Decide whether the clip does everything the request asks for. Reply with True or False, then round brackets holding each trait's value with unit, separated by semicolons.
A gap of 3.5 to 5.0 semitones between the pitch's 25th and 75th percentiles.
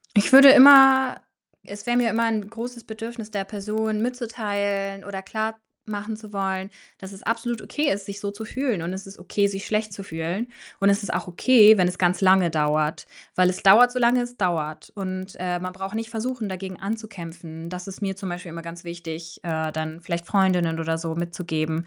True (3.9 semitones)